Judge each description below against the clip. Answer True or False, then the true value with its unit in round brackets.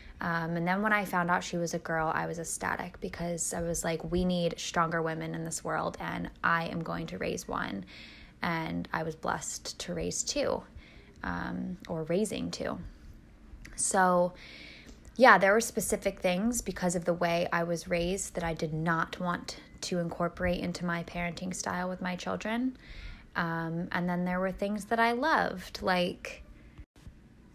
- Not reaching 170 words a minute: False (175 wpm)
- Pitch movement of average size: False (2.0 semitones)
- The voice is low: False (175 Hz)